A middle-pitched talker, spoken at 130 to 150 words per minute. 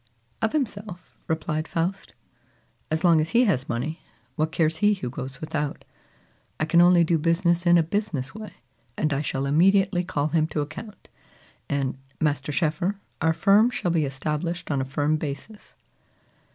No: medium, 160 Hz; average, 165 wpm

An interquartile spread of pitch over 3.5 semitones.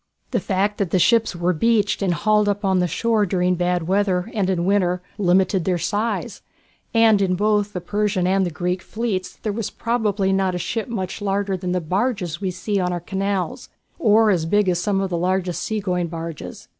No: narrow, 2.6 semitones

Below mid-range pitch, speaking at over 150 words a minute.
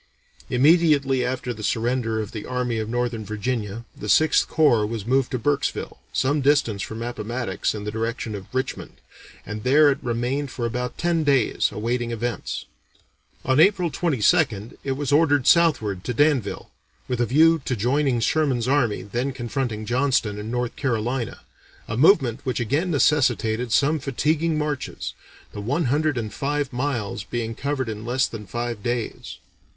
Yes: low, 125 Hz; average, 160 wpm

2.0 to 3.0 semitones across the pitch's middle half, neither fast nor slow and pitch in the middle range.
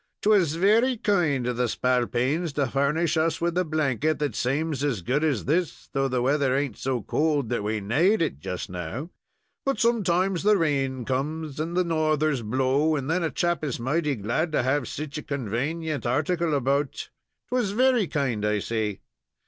No: average, 4.6 semitones; average, 180 wpm; medium, 145 Hz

